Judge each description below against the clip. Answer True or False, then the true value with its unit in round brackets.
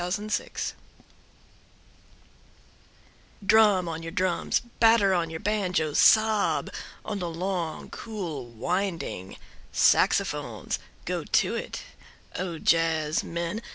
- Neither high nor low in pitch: True (180 Hz)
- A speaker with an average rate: False (95 wpm)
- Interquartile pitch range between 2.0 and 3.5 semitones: False (3.9 semitones)